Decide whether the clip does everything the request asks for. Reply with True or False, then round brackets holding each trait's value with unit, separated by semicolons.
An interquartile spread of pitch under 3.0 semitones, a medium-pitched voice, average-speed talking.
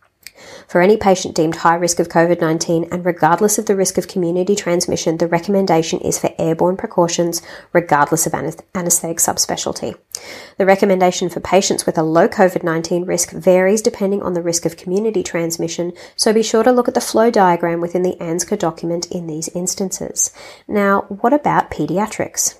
True (2.5 semitones; 180 Hz; 175 wpm)